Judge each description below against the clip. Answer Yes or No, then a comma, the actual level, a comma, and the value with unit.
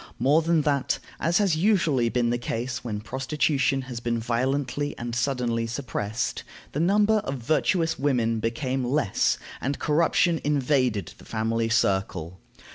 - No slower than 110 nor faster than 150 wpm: Yes, average, 140 wpm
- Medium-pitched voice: No, low, 130 Hz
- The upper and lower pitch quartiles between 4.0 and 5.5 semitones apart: Yes, average, 4.3 semitones